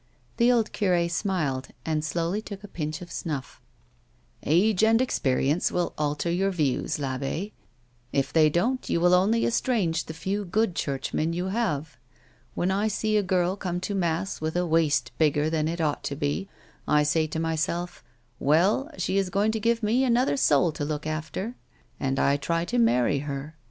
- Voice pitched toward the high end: No, medium, 170 Hz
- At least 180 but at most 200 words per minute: Yes, average, 190 wpm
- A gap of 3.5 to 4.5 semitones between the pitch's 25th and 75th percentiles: No, average, 4.9 semitones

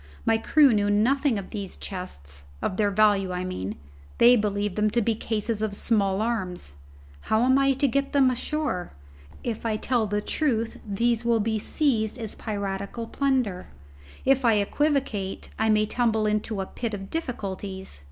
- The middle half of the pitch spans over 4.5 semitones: No, average, 3.3 semitones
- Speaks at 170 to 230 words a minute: No, average, 160 wpm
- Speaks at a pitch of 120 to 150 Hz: No, high, 215 Hz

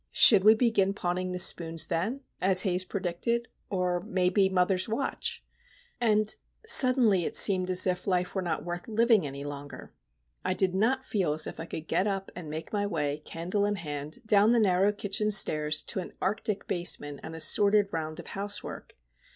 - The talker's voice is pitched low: No, medium, 185 Hz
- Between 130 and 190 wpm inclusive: Yes, average, 175 wpm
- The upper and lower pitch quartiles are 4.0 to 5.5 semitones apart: No, average, 3.3 semitones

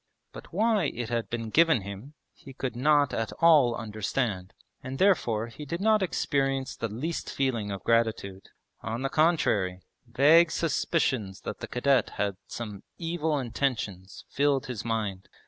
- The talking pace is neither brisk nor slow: Yes, average, 150 wpm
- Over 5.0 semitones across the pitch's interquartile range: Yes, wide, 5.6 semitones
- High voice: No, low, 125 Hz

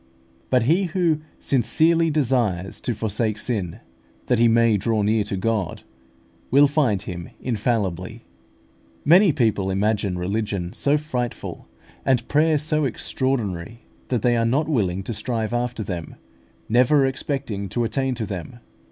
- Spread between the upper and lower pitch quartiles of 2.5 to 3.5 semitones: No, average, 4.8 semitones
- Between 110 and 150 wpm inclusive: Yes, average, 140 wpm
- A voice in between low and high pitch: No, low, 115 Hz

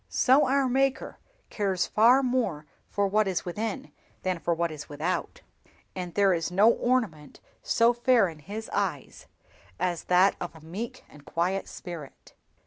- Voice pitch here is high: Yes, high, 195 Hz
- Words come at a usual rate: Yes, average, 155 wpm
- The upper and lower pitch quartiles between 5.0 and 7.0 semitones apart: Yes, wide, 5.5 semitones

